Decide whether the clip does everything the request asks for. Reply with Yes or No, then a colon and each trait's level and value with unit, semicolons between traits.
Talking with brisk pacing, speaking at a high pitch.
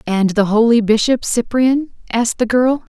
No: average, 165 wpm; high, 235 Hz